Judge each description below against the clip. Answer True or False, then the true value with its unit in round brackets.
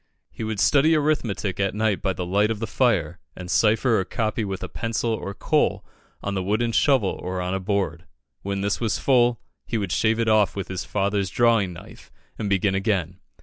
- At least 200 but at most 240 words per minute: True (205 wpm)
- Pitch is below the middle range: True (100 Hz)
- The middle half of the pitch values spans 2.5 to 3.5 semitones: True (3.0 semitones)